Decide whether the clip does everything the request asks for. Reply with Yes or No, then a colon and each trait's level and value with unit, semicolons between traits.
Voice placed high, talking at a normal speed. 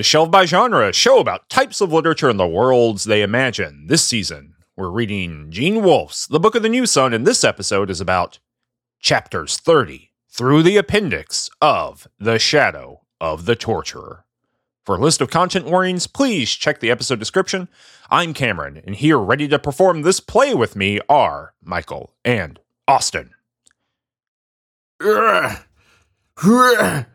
No: low, 130 Hz; average, 155 wpm